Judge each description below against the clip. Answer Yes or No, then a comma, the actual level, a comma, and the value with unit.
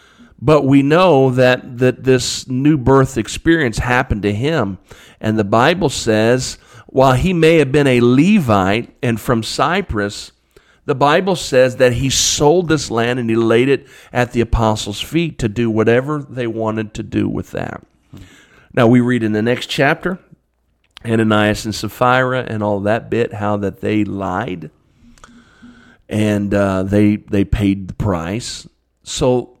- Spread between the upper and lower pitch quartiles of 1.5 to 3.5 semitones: No, average, 3.9 semitones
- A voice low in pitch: Yes, low, 120 Hz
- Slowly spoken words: No, average, 155 wpm